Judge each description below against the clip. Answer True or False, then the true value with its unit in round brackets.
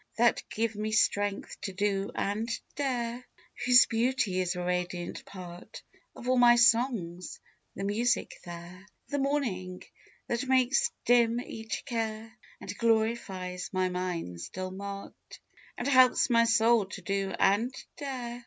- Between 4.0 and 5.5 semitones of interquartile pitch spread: True (4.4 semitones)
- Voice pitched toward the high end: True (220 Hz)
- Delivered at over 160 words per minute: False (135 wpm)